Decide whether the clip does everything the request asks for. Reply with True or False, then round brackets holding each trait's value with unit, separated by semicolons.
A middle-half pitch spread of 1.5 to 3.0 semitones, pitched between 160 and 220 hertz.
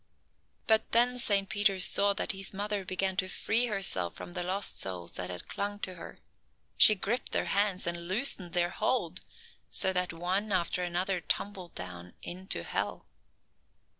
True (2.7 semitones; 190 Hz)